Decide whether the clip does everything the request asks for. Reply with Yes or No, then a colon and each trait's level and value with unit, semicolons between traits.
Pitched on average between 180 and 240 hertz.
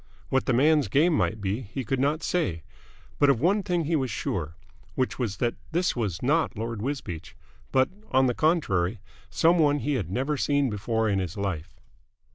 No: low, 130 Hz